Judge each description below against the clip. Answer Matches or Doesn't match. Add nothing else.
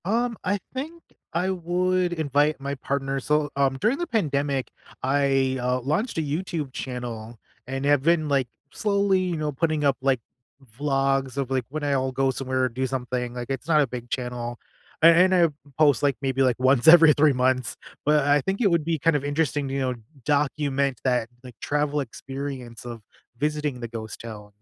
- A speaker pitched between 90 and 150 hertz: Matches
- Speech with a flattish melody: Doesn't match